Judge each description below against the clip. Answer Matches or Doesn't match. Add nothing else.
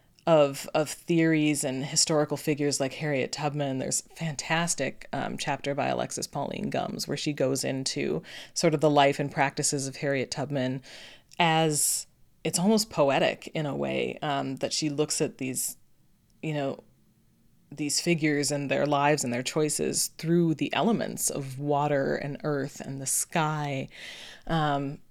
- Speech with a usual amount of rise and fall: Doesn't match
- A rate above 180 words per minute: Doesn't match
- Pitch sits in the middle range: Matches